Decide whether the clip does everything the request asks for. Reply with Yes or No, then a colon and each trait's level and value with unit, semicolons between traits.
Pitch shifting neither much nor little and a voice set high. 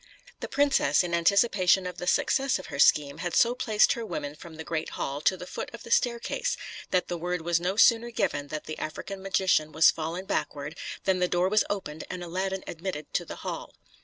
No: average, 3.7 semitones; medium, 180 Hz